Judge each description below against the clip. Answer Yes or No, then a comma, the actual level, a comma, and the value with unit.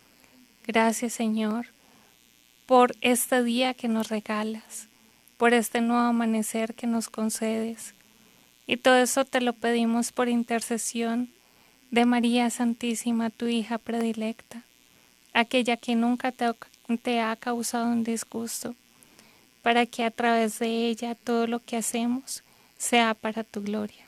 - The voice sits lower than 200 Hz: No, high, 235 Hz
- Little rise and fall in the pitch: Yes, narrow, 1.1 semitones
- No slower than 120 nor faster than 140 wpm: Yes, average, 130 wpm